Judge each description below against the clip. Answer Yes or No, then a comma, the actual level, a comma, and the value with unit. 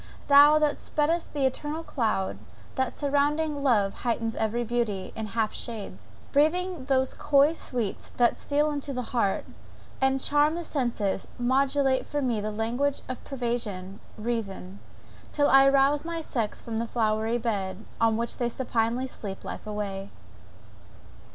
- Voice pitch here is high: Yes, high, 245 Hz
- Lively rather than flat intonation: No, average, 4.4 semitones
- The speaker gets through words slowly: No, average, 145 wpm